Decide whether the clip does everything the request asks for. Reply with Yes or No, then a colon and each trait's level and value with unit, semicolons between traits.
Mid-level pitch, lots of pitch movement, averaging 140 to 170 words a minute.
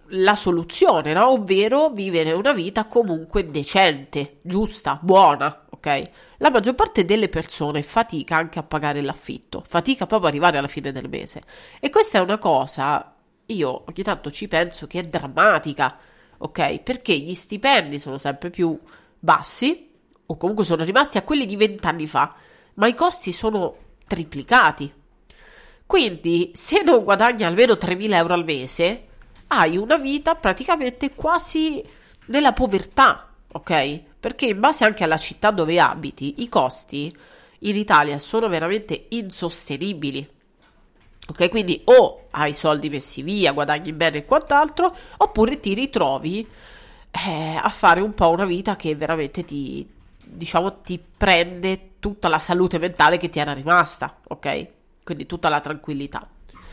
Yes: medium, 180 Hz; wide, 6.1 semitones; average, 145 wpm